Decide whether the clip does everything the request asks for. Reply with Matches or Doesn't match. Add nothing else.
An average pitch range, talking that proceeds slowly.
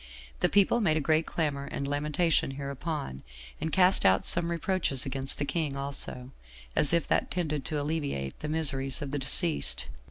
Doesn't match